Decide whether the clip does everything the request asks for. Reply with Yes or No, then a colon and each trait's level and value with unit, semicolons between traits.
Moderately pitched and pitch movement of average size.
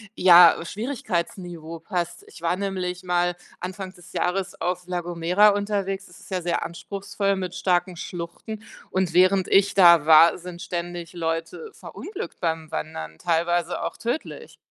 No: medium, 180 Hz; narrow, 2.3 semitones